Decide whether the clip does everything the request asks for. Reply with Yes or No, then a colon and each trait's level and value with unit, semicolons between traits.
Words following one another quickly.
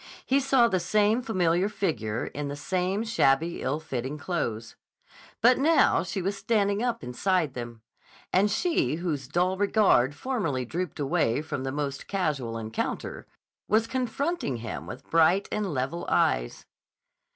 No: average, 145 wpm